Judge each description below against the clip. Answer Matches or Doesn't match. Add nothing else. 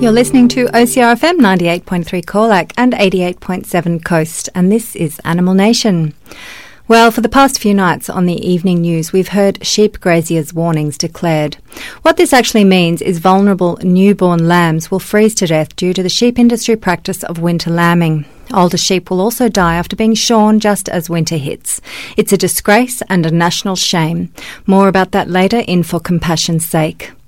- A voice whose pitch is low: Doesn't match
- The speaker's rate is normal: Matches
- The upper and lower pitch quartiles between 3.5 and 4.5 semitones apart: Matches